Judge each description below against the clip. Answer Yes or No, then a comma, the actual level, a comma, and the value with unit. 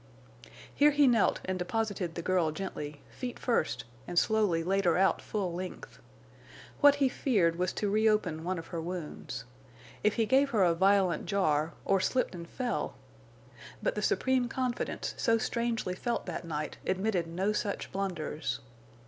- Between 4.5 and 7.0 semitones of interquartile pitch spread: Yes, average, 5.1 semitones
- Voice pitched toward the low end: No, high, 190 Hz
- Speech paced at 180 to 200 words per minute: No, average, 160 wpm